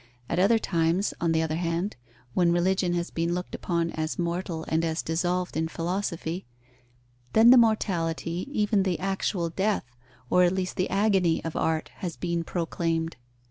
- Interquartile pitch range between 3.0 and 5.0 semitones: No, narrow, 2.4 semitones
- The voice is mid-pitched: Yes, medium, 175 Hz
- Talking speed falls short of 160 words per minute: No, average, 165 wpm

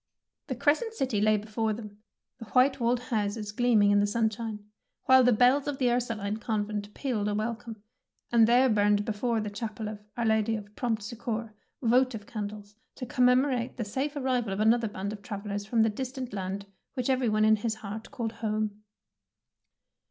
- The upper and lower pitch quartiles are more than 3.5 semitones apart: No, average, 2.8 semitones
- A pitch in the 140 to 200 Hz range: No, high, 220 Hz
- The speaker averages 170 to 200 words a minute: Yes, average, 180 wpm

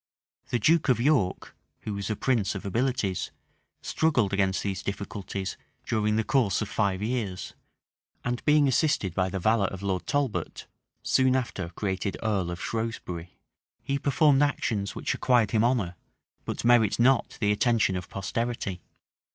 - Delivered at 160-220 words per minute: No, average, 150 wpm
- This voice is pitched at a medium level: No, low, 110 Hz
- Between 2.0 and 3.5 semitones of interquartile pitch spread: No, average, 4.4 semitones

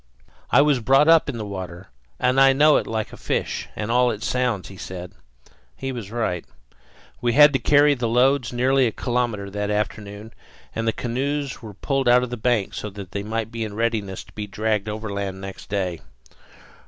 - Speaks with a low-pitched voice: Yes, low, 115 Hz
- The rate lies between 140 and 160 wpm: No, average, 200 wpm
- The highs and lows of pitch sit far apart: No, average, 3.8 semitones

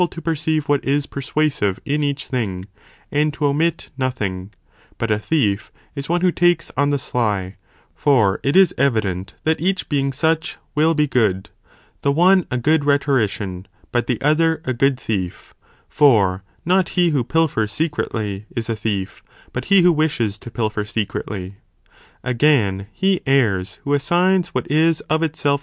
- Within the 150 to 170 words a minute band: Yes, average, 160 wpm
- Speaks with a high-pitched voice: No, medium, 140 Hz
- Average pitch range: No, wide, 6.8 semitones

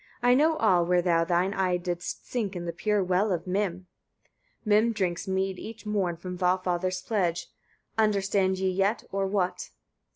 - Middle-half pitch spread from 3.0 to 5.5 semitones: No, narrow, 2.5 semitones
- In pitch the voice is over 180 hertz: Yes, high, 190 Hz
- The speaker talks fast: No, average, 165 wpm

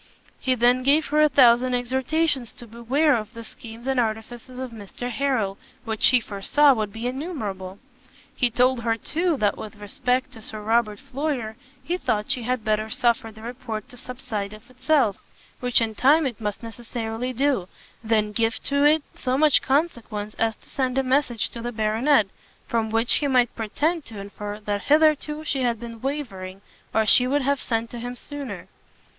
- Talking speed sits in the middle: Yes, average, 185 wpm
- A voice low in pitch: No, high, 240 Hz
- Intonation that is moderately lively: Yes, average, 3.5 semitones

